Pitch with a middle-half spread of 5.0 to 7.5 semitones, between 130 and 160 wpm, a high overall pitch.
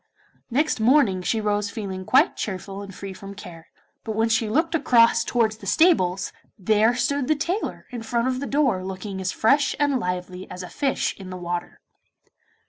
No: average, 5.3 semitones; average, 185 wpm; high, 220 Hz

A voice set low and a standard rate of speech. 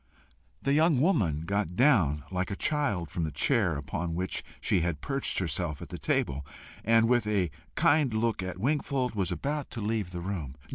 Yes: low, 100 Hz; average, 185 wpm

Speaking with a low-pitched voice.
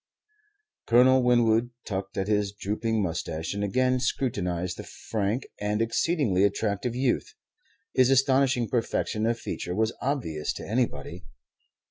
Yes: low, 110 Hz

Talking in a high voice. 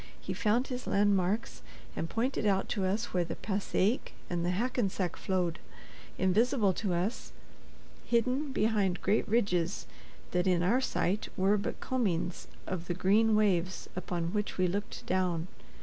Yes: high, 195 Hz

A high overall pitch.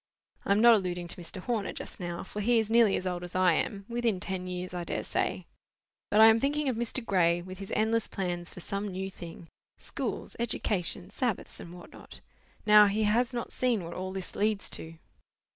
Yes: high, 195 Hz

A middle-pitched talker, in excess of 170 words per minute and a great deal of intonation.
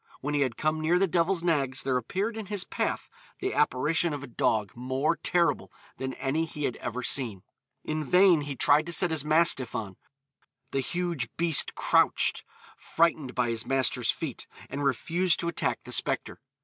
No: medium, 150 Hz; average, 180 wpm; average, 4.6 semitones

